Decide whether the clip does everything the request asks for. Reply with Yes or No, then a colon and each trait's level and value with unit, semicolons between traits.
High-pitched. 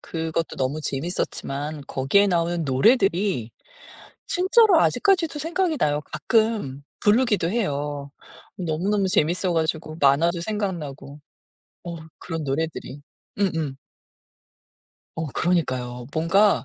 No: medium, 165 Hz